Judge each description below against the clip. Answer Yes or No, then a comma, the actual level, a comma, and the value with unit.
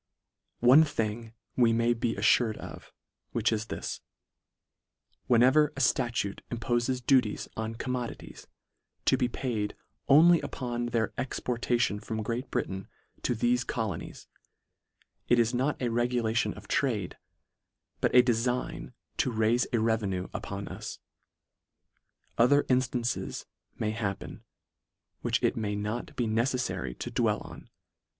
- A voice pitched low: Yes, low, 120 Hz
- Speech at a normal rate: No, slow, 130 wpm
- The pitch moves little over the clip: Yes, narrow, 2.1 semitones